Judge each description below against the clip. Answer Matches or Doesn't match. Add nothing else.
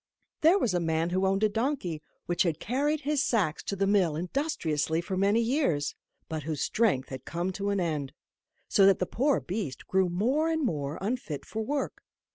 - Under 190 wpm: Doesn't match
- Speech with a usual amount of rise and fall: Doesn't match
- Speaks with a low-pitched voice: Doesn't match